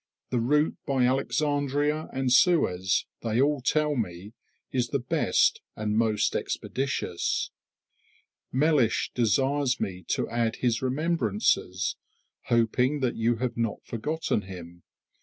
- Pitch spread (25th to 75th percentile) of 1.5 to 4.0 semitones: No, average, 4.7 semitones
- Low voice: Yes, low, 125 Hz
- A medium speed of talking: No, slow, 115 wpm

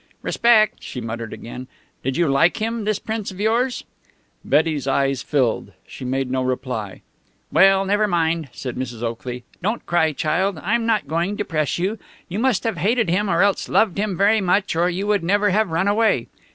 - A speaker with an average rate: Yes, average, 190 wpm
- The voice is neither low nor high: Yes, medium, 180 Hz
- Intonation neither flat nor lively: No, wide, 7.3 semitones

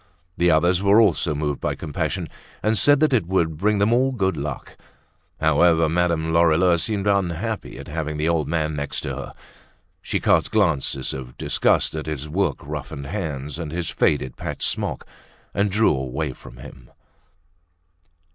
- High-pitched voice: No, very low, 80 Hz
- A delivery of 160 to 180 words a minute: Yes, average, 165 wpm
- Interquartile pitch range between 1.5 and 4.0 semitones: No, average, 4.6 semitones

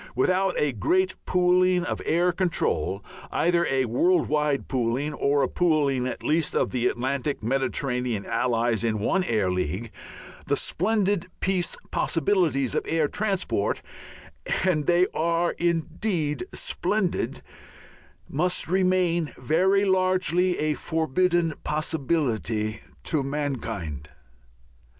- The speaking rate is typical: No, slow, 115 wpm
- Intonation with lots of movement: Yes, wide, 6.1 semitones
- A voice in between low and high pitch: Yes, medium, 155 Hz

